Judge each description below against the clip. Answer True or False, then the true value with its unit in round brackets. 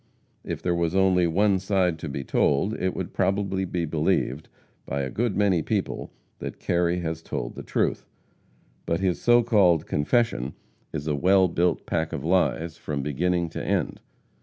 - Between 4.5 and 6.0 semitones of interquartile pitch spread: False (3.2 semitones)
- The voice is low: True (85 Hz)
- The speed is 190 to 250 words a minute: False (170 wpm)